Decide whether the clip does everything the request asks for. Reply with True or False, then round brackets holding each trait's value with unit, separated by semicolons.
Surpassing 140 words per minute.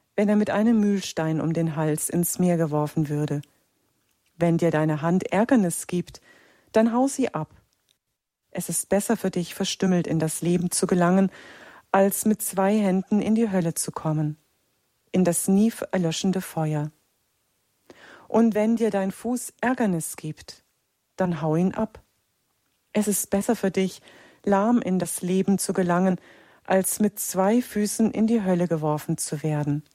True (160 wpm)